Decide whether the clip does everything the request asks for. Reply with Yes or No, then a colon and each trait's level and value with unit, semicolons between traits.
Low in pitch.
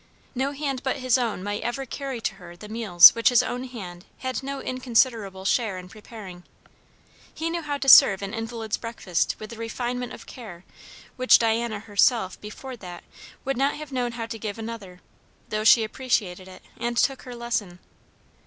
No: high, 230 Hz